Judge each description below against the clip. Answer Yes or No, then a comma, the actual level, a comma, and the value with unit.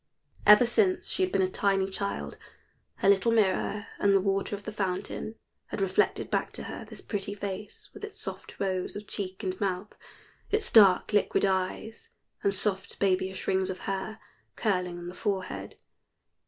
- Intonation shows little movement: Yes, narrow, 1.9 semitones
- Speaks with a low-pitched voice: No, high, 195 Hz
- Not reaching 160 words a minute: No, average, 170 wpm